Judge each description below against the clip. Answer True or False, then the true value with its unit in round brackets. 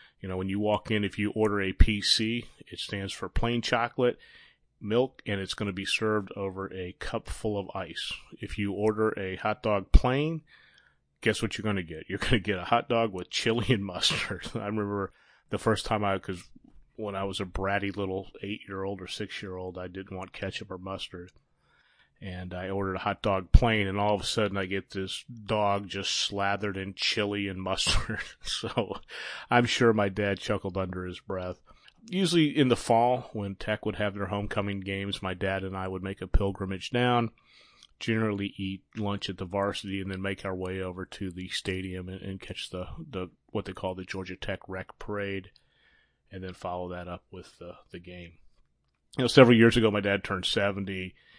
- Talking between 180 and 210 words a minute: True (205 wpm)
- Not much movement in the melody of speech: True (2.1 semitones)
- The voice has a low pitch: True (100 Hz)